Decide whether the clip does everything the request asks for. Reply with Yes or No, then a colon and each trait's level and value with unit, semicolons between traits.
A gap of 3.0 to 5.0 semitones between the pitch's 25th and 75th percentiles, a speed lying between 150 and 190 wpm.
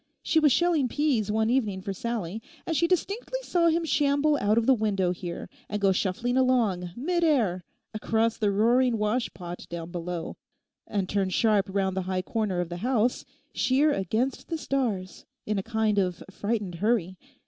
No: wide, 5.5 semitones; average, 170 wpm